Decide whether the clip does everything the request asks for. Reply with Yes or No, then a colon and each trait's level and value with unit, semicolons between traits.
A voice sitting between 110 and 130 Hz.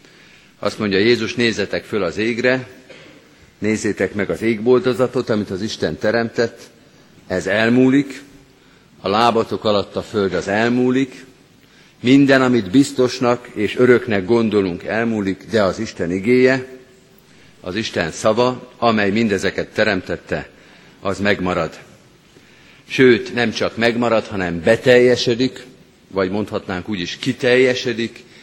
Yes: low, 115 Hz